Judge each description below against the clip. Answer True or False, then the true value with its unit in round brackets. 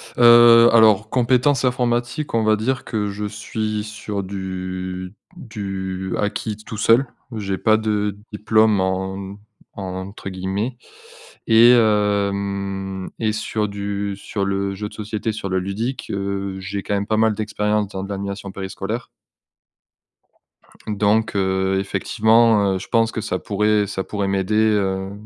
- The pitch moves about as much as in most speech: False (2.1 semitones)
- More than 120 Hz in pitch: False (105 Hz)